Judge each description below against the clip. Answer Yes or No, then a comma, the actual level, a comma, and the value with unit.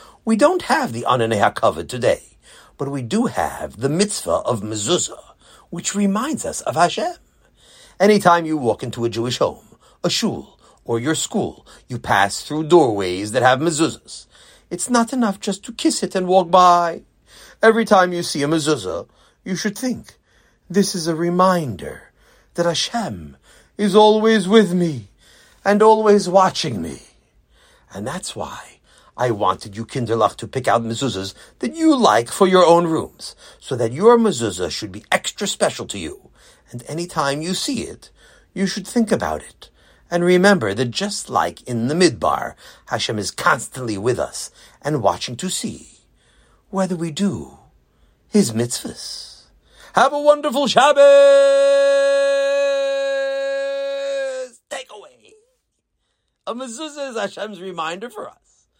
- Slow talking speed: No, average, 150 wpm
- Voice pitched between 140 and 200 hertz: Yes, high, 190 Hz